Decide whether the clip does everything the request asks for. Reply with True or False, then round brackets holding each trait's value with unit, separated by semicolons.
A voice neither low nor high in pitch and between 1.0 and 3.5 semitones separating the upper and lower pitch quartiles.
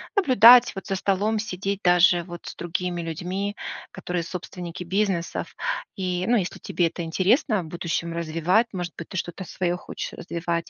True (180 Hz; 2.5 semitones)